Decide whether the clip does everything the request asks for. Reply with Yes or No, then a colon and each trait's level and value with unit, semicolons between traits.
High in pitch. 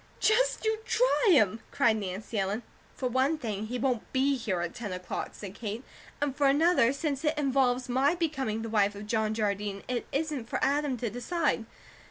Yes: very high, 250 Hz